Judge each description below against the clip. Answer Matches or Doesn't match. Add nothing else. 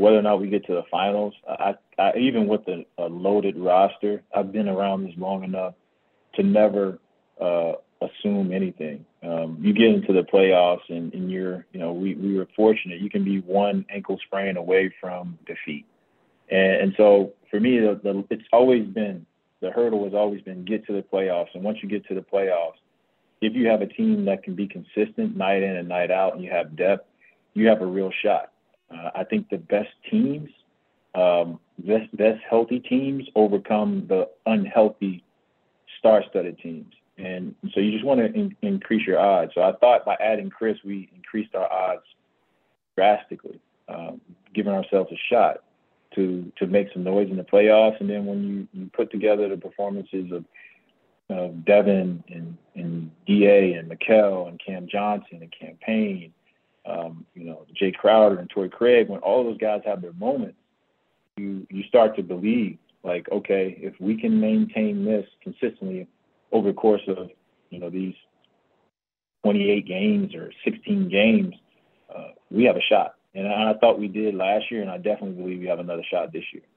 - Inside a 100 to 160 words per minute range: Doesn't match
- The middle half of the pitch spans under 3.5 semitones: Matches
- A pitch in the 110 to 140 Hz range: Doesn't match